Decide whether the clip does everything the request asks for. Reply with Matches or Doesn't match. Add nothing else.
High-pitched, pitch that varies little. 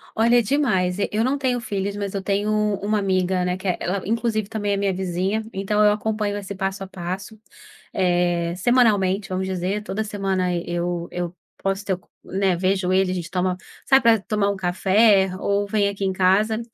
Matches